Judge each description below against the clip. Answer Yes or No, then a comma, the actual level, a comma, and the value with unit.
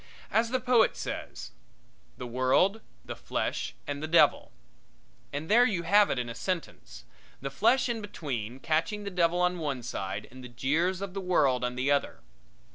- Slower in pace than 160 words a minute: No, average, 180 wpm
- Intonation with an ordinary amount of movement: No, wide, 7.6 semitones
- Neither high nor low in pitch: Yes, medium, 160 Hz